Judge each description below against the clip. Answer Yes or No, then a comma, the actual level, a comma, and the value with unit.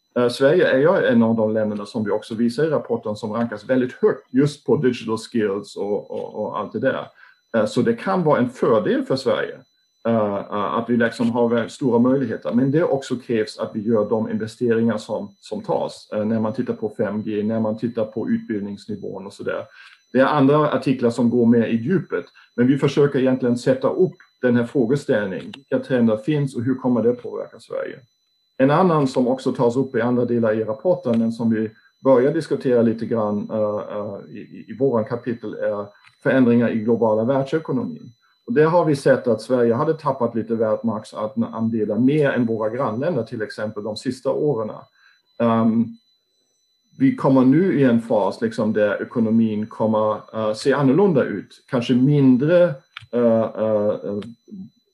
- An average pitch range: Yes, average, 4.0 semitones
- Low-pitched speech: Yes, low, 120 Hz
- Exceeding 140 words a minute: Yes, average, 175 wpm